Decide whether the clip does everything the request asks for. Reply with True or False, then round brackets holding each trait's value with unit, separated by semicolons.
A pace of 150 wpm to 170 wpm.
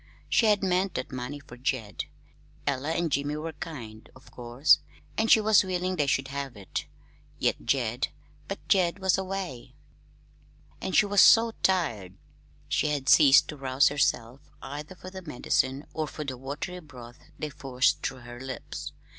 True (165 wpm)